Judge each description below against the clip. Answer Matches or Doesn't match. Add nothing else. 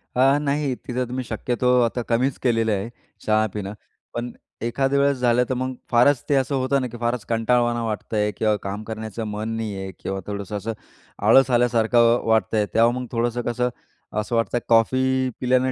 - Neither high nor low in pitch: Doesn't match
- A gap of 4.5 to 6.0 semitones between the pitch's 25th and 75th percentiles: Doesn't match